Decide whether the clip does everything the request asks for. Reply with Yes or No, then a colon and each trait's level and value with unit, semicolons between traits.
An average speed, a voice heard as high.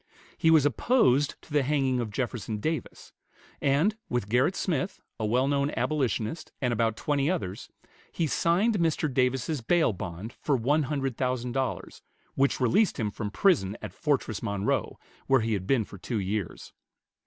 No: average, 165 wpm; low, 130 Hz